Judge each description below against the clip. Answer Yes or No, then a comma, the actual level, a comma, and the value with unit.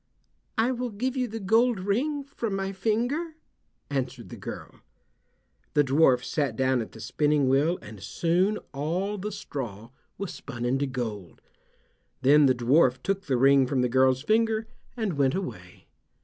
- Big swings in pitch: Yes, wide, 8.5 semitones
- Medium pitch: Yes, medium, 150 Hz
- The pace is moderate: Yes, average, 160 wpm